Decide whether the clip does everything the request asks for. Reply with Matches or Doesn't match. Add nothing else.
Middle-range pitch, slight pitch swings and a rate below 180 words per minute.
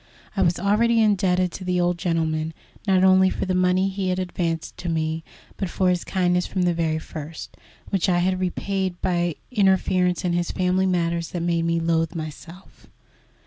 Doesn't match